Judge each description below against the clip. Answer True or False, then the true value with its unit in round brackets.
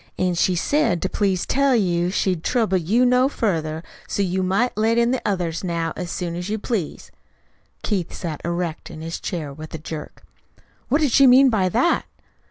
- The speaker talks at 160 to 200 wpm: True (190 wpm)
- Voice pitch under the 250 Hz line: True (185 Hz)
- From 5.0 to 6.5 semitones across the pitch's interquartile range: True (5.6 semitones)